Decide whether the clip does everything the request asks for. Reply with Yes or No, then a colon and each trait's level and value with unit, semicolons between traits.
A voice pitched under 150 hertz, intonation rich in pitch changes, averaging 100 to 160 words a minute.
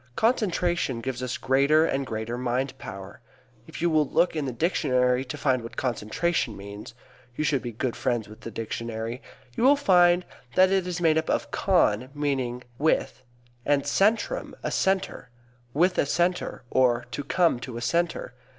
No: low, 135 Hz; wide, 6.3 semitones; average, 170 wpm